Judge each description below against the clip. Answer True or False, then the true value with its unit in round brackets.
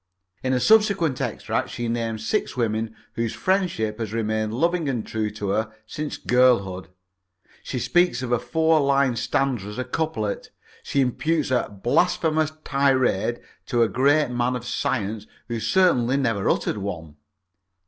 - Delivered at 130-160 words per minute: True (150 wpm)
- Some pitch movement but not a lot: True (4.3 semitones)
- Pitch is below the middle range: True (120 Hz)